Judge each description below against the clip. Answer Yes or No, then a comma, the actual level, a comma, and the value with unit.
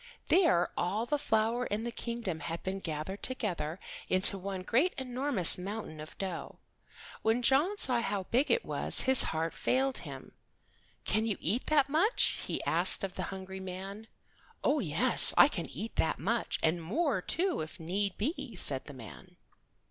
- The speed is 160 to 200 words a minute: Yes, average, 170 wpm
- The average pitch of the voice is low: No, high, 205 Hz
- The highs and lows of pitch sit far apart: Yes, wide, 5.9 semitones